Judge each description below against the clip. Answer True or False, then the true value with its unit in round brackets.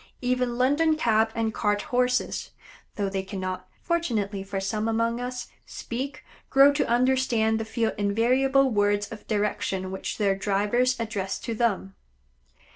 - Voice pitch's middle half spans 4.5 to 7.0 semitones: False (3.6 semitones)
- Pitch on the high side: True (225 Hz)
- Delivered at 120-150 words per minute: True (140 wpm)